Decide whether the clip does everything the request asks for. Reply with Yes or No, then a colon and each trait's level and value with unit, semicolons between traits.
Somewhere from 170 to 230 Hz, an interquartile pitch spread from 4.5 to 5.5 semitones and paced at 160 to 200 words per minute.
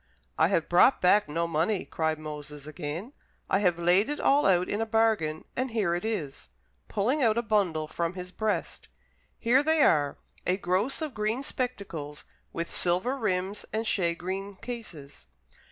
Yes: high, 190 Hz; average, 5.1 semitones; average, 165 wpm